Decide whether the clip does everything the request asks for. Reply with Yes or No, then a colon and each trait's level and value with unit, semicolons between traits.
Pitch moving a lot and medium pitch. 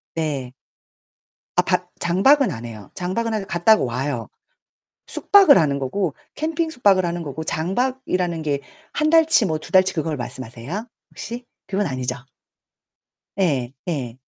Yes: wide, 8.0 semitones; medium, 175 Hz